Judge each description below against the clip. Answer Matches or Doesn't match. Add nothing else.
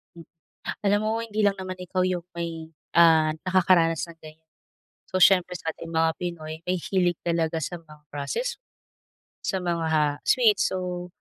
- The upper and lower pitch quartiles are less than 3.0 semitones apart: Matches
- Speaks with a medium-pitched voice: Matches